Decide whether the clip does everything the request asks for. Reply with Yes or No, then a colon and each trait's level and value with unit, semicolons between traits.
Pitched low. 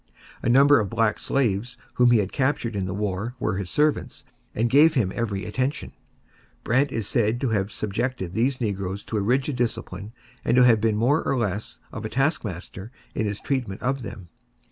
Yes: low, 115 Hz